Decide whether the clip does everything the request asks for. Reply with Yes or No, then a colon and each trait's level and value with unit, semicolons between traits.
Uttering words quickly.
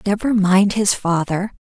No: average, 145 wpm